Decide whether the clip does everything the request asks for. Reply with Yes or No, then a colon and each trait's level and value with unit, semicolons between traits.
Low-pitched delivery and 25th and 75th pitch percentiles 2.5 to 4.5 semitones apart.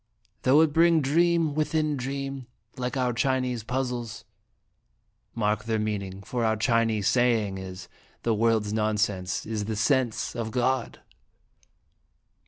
Yes: low, 115 Hz; average, 3.6 semitones